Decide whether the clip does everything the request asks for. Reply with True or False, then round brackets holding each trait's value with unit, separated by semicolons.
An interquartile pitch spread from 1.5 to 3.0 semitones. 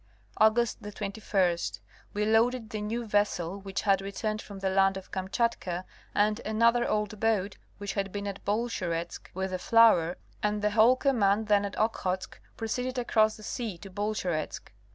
True (2.4 semitones)